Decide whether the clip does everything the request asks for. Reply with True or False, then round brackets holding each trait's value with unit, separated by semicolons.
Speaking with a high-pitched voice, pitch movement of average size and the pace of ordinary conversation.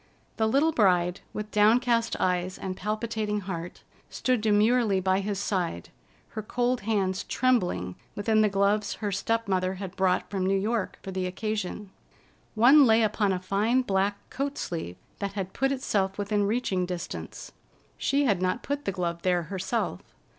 True (200 Hz; 3.2 semitones; 160 wpm)